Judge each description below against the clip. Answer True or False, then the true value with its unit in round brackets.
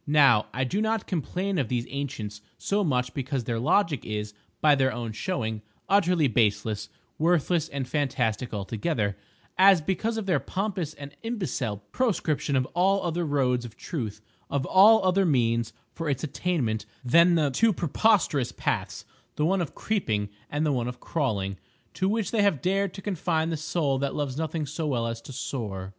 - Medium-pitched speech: True (145 Hz)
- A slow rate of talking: False (170 wpm)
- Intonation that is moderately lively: False (6.9 semitones)